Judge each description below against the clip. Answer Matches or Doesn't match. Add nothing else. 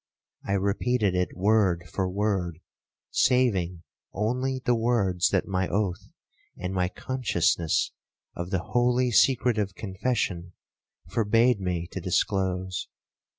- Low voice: Matches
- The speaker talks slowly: Matches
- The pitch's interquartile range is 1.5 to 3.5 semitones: Doesn't match